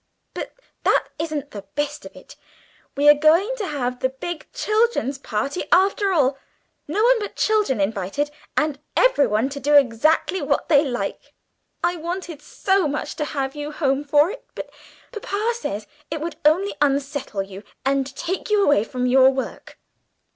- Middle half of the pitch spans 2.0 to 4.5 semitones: No, average, 5.2 semitones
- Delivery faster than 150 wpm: Yes, average, 165 wpm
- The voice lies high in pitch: Yes, very high, 295 Hz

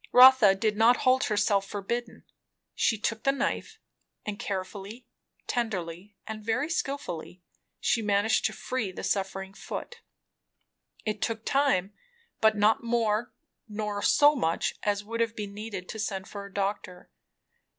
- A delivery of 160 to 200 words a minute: No, average, 140 wpm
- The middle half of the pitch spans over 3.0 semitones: No, narrow, 2.6 semitones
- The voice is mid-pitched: No, high, 210 Hz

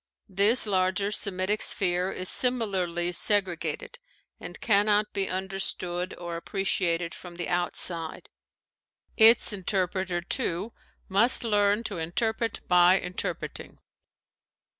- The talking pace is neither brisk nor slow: No, slow, 100 wpm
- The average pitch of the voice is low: No, high, 190 Hz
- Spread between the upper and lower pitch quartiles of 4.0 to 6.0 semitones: No, average, 2.8 semitones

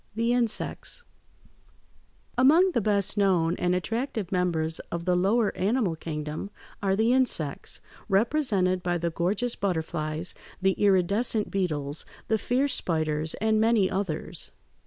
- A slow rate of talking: Yes, slow, 125 wpm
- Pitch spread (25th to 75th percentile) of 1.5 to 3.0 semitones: No, average, 4.9 semitones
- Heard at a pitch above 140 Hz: Yes, high, 190 Hz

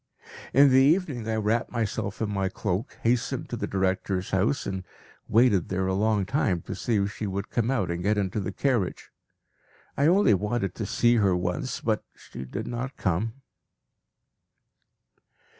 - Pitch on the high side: No, low, 105 Hz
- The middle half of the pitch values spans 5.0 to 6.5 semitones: No, average, 4.0 semitones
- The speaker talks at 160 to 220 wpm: Yes, average, 170 wpm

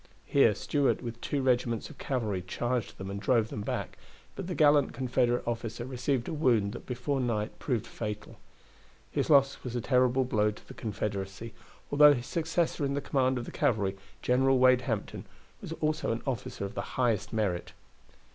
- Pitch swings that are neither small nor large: Yes, average, 3.8 semitones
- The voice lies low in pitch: Yes, low, 120 Hz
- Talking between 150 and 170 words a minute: No, average, 180 wpm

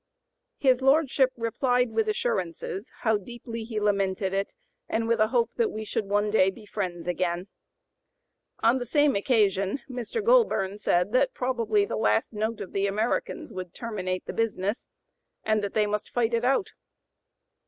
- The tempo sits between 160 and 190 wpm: Yes, average, 165 wpm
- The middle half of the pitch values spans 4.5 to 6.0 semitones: No, average, 3.6 semitones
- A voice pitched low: No, high, 220 Hz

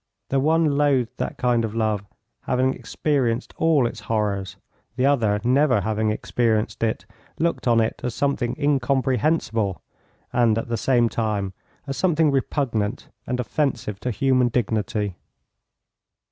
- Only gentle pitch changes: No, average, 3.8 semitones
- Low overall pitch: Yes, low, 120 Hz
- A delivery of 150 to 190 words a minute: No, slow, 135 wpm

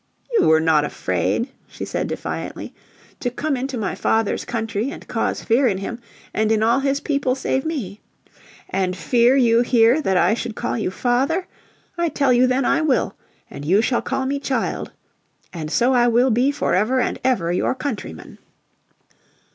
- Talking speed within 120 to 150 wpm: No, average, 175 wpm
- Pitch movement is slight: No, average, 4.3 semitones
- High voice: Yes, high, 240 Hz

